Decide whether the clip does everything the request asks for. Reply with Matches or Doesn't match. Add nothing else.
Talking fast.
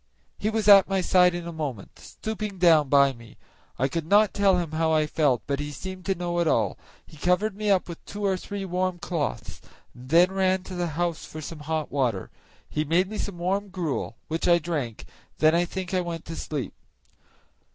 Matches